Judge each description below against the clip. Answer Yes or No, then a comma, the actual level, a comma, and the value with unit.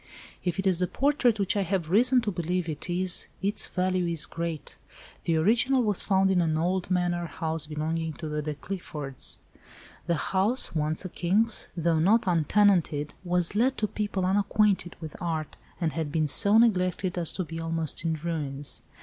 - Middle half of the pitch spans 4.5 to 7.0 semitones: No, average, 3.6 semitones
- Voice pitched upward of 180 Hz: No, medium, 175 Hz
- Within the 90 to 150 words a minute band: No, average, 175 wpm